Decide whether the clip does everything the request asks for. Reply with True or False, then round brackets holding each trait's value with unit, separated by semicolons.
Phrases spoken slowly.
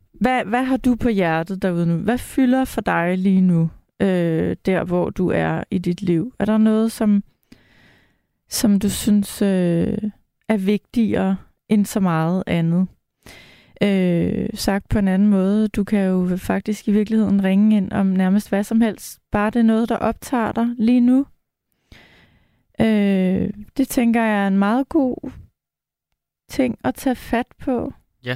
False (165 wpm)